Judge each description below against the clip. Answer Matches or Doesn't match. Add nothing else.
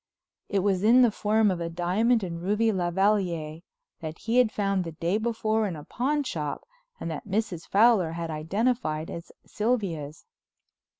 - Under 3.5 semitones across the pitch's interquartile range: Doesn't match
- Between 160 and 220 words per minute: Matches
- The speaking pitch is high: Matches